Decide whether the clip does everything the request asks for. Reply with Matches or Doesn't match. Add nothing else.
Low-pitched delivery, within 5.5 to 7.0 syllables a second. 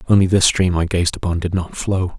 Matches